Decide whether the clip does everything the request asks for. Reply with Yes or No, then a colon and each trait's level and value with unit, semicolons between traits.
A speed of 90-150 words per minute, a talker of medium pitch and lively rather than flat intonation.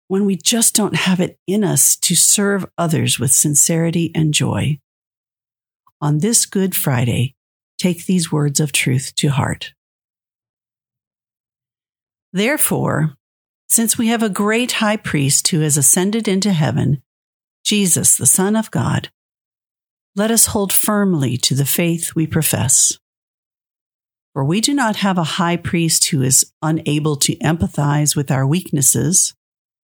Yes: average, 140 wpm; medium, 155 Hz; wide, 5.8 semitones